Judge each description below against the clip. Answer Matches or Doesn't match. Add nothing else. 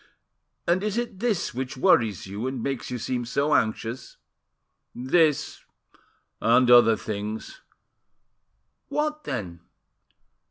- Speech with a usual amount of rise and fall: Doesn't match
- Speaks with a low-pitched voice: Matches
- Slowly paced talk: Matches